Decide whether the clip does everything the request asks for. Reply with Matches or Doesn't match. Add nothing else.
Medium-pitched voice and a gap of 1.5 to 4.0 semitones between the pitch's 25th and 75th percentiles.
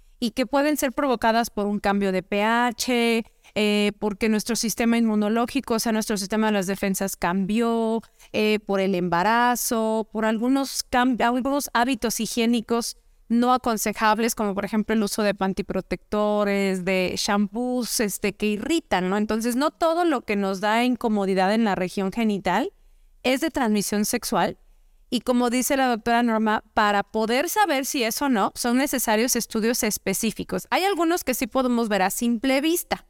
Doesn't match